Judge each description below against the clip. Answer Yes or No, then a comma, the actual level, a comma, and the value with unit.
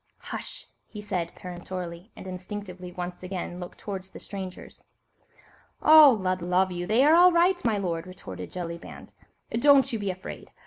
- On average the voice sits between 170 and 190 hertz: Yes, medium, 185 Hz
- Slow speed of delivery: No, average, 160 wpm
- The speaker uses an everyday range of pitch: Yes, average, 3.6 semitones